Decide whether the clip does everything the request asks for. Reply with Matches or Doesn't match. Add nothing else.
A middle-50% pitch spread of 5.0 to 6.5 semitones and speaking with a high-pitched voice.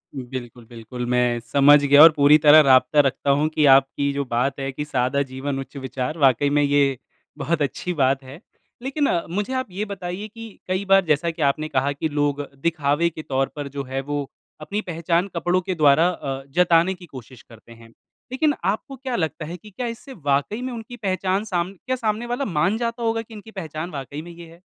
Doesn't match